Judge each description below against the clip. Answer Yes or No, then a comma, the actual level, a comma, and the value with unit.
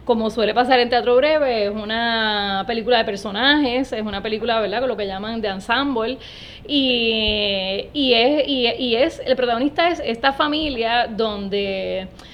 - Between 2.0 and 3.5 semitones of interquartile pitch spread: Yes, average, 3.2 semitones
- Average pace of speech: Yes, average, 160 wpm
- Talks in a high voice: Yes, high, 230 Hz